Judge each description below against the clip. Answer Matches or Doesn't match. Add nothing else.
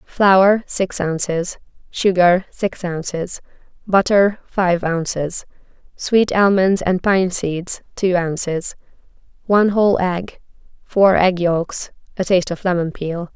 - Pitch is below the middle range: Doesn't match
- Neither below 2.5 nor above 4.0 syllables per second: Matches